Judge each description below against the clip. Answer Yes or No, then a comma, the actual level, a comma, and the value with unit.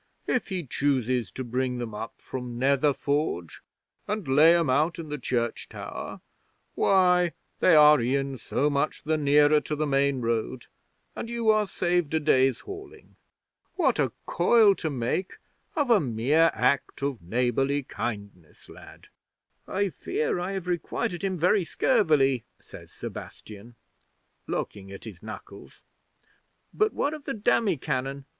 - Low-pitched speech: No, medium, 145 Hz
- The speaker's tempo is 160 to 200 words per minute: No, average, 150 wpm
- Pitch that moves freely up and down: Yes, wide, 6.1 semitones